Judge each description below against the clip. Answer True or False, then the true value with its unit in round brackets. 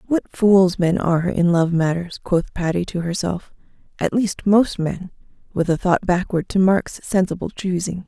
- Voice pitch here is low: False (180 Hz)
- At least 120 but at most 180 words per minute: True (165 wpm)